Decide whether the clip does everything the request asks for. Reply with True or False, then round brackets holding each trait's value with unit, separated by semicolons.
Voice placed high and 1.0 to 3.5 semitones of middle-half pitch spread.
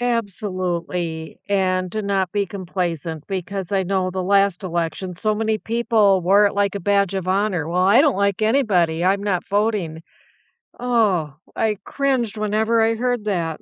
True (195 Hz; 3.0 semitones)